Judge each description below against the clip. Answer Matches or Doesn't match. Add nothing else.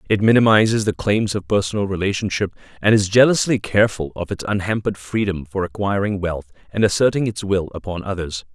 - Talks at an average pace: Matches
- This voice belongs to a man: Matches